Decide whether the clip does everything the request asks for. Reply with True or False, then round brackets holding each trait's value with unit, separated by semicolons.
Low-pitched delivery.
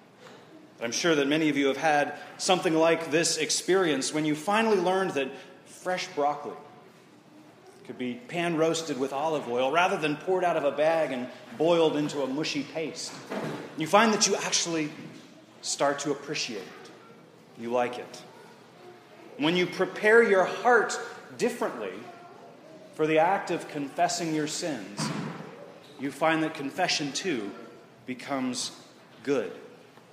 False (155 Hz)